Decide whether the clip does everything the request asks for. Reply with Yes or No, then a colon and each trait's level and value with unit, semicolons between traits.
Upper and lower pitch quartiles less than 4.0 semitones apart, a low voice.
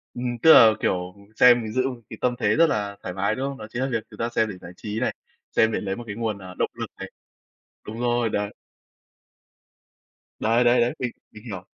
Yes: average, 3.0 semitones; low, 115 Hz